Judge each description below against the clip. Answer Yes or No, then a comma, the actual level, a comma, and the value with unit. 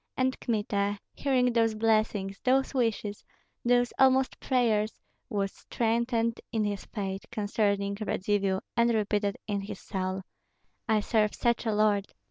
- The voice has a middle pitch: No, high, 215 Hz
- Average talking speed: No, slow, 130 wpm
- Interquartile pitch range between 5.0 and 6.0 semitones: No, average, 2.7 semitones